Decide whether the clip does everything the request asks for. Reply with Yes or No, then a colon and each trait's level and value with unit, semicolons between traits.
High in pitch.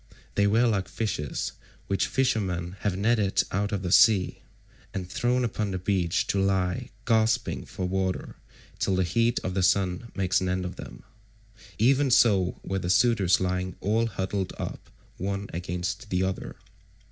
No: very low, 95 Hz